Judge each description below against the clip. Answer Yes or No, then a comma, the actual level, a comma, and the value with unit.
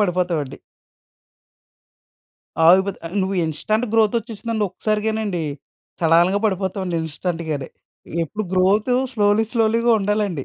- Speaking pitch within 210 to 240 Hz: No, high, 195 Hz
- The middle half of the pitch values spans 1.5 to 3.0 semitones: No, average, 3.6 semitones